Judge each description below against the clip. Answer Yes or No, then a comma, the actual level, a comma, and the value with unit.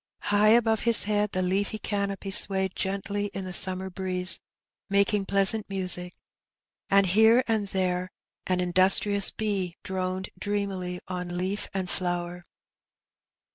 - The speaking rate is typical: No, slow, 130 wpm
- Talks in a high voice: Yes, high, 195 Hz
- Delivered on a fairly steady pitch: Yes, narrow, 1.9 semitones